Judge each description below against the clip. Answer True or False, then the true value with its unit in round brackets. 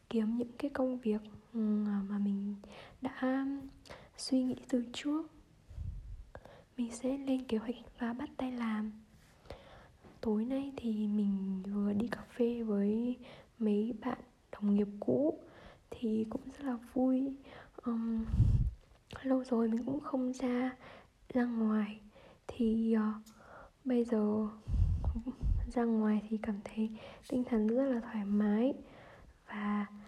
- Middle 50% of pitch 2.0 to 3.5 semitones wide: True (3.1 semitones)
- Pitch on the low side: False (230 Hz)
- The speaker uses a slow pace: True (125 wpm)